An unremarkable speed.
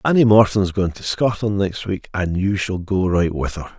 No: fast, 240 wpm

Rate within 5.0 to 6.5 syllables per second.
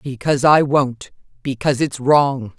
No: 4.6 syllables/s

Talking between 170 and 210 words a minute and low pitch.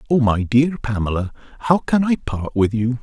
Yes: average, 200 wpm; low, 125 Hz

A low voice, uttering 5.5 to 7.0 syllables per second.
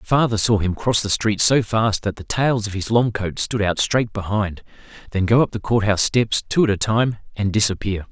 No: low, 105 Hz; 5.0 syllables/s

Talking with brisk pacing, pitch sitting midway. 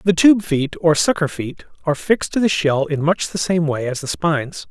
Yes: fast, 245 wpm; medium, 160 Hz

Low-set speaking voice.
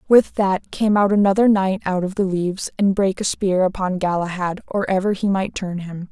No: high, 190 Hz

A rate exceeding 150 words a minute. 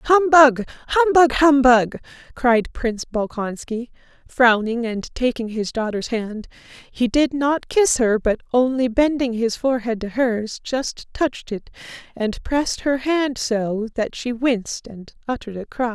No: average, 145 wpm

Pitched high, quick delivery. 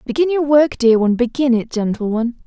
Yes: very high, 250 Hz; fast, 220 wpm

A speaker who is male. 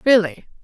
No: female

